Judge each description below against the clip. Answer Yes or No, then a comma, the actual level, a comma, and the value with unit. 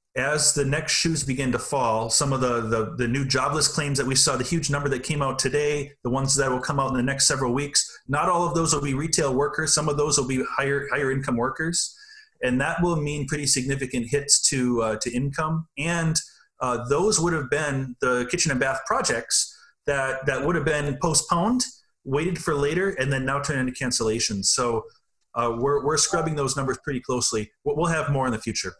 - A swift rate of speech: Yes, fast, 220 wpm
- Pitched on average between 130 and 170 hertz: Yes, medium, 140 Hz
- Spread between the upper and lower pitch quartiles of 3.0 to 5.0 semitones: Yes, average, 3.4 semitones